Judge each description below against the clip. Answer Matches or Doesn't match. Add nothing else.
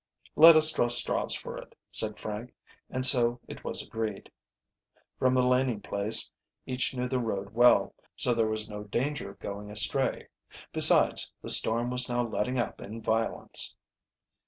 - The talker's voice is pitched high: Doesn't match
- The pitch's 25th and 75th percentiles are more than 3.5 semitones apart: Doesn't match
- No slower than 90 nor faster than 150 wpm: Doesn't match